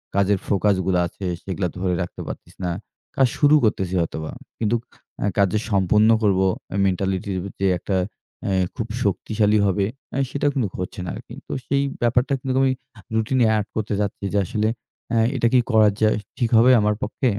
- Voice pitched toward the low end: Yes, low, 105 Hz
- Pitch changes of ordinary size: Yes, average, 3.2 semitones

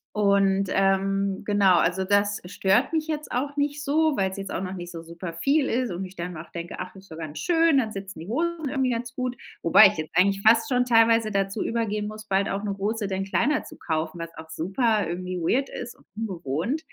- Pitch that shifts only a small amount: No, average, 5.0 semitones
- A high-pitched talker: Yes, high, 200 Hz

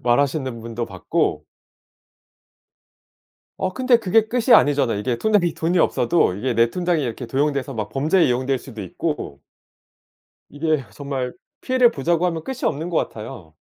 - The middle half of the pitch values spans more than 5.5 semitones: Yes, wide, 6.4 semitones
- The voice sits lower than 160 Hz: Yes, medium, 140 Hz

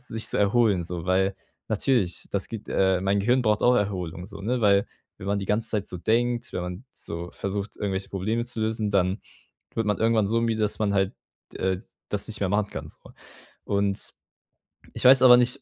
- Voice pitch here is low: Yes, low, 100 Hz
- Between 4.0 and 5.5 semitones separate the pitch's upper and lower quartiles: No, average, 2.7 semitones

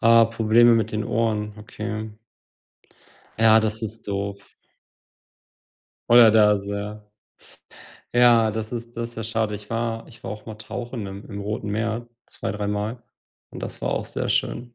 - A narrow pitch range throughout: Yes, narrow, 1.6 semitones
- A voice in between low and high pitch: No, low, 110 Hz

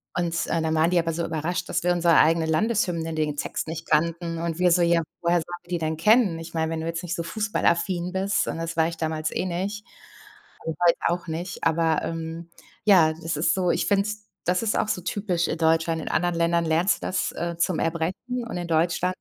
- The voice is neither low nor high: Yes, medium, 170 Hz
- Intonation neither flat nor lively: No, narrow, 1.8 semitones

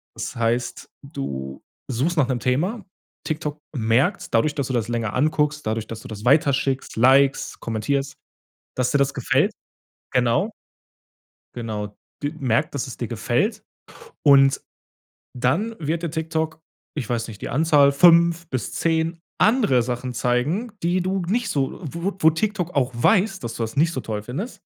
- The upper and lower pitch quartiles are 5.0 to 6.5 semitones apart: Yes, wide, 5.6 semitones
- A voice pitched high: No, medium, 140 Hz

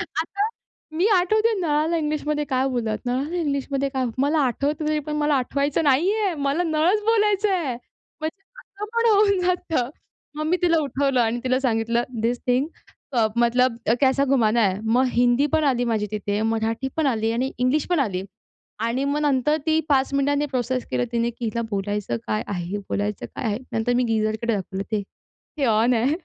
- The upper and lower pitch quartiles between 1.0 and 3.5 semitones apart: No, average, 4.8 semitones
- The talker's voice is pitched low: No, very high, 265 Hz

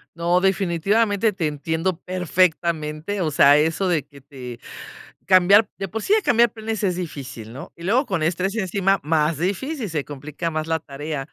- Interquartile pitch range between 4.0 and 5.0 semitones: Yes, average, 4.4 semitones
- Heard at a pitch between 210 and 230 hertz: No, medium, 170 Hz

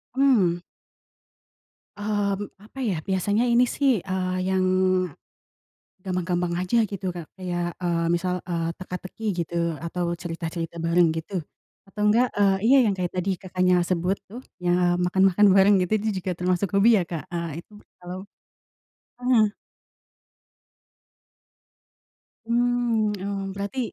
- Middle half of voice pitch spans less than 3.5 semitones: Yes, average, 2.9 semitones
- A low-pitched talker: No, medium, 185 Hz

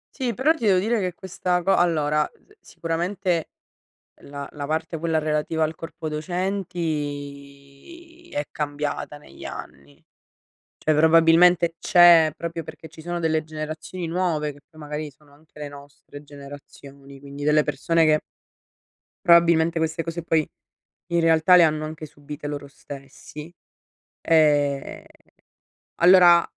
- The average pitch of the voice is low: No, medium, 160 Hz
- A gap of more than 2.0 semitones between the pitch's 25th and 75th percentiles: Yes, narrow, 2.6 semitones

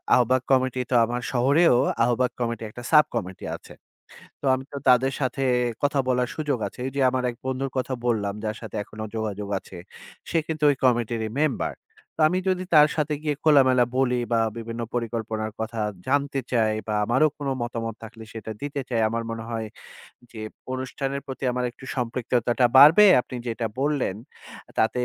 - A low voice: Yes, low, 125 Hz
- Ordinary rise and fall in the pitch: Yes, average, 3.1 semitones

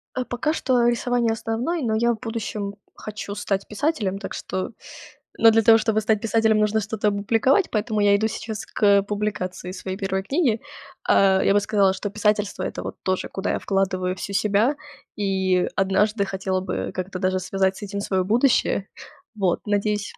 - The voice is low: No, high, 205 Hz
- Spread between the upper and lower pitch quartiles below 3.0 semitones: Yes, narrow, 2.6 semitones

